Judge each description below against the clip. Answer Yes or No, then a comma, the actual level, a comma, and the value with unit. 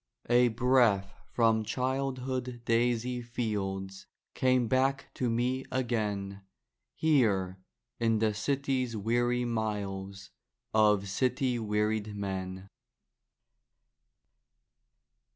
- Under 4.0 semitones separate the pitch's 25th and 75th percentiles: Yes, average, 3.6 semitones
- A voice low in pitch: Yes, low, 115 Hz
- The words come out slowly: Yes, slow, 85 wpm